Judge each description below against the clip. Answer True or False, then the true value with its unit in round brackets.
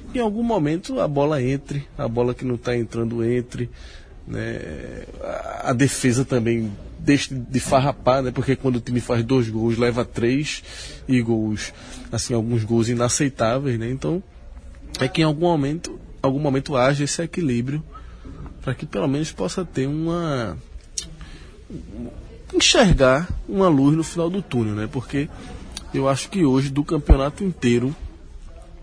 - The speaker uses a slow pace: False (150 wpm)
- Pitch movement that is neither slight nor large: True (3.8 semitones)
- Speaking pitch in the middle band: False (130 Hz)